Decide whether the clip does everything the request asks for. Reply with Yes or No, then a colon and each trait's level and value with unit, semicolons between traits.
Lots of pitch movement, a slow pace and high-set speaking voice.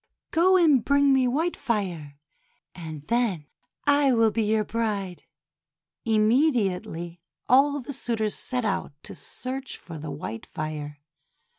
Yes: wide, 7.5 semitones; slow, 130 wpm; high, 225 Hz